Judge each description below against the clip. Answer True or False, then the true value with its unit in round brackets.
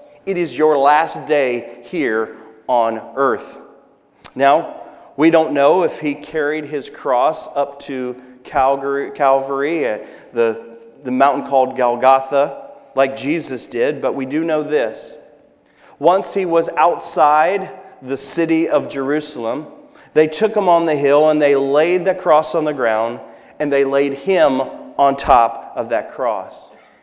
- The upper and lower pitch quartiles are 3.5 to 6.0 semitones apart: False (2.7 semitones)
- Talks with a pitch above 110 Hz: True (140 Hz)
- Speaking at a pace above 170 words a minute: False (145 wpm)